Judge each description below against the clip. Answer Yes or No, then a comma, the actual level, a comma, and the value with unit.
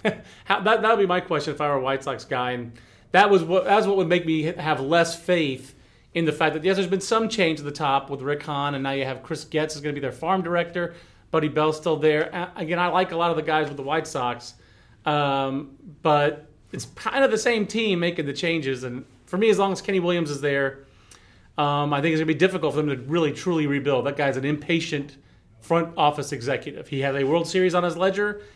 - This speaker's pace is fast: Yes, fast, 255 wpm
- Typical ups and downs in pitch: Yes, average, 4.1 semitones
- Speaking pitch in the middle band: Yes, medium, 155 Hz